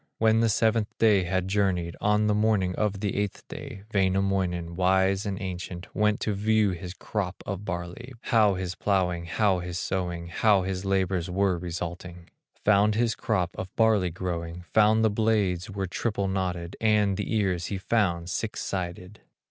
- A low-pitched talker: Yes, very low, 95 Hz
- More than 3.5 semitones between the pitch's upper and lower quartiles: No, average, 2.9 semitones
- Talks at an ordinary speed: Yes, average, 165 wpm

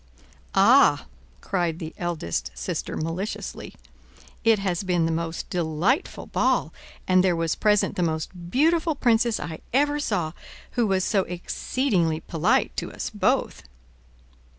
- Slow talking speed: Yes, slow, 130 wpm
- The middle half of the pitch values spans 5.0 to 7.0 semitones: Yes, wide, 5.4 semitones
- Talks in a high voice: No, medium, 180 Hz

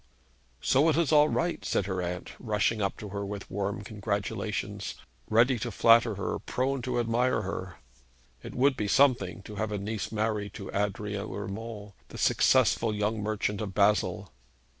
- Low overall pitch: Yes, low, 105 Hz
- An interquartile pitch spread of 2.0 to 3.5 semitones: Yes, narrow, 2.6 semitones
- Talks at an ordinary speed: Yes, average, 165 wpm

